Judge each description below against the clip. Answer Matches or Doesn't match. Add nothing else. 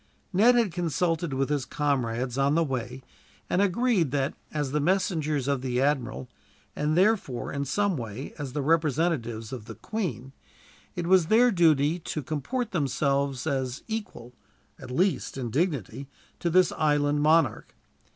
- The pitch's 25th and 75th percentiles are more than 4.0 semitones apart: Matches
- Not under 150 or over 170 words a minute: Matches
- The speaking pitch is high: Doesn't match